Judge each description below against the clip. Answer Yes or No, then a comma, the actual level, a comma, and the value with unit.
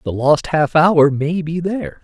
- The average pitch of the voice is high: No, medium, 155 Hz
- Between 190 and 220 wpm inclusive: Yes, fast, 205 wpm